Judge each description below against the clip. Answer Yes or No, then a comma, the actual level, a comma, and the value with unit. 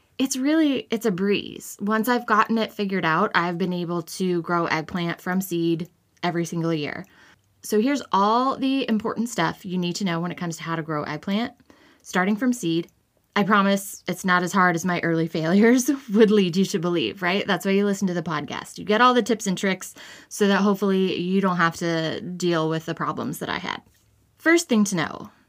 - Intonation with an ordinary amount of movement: Yes, average, 4.1 semitones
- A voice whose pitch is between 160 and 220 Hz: Yes, high, 190 Hz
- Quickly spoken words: Yes, fast, 215 wpm